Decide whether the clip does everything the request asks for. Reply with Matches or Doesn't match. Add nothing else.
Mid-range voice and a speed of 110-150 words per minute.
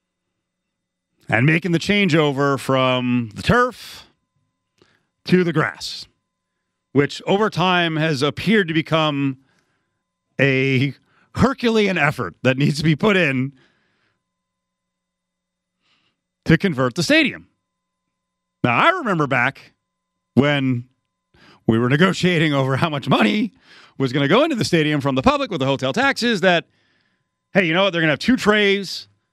Matches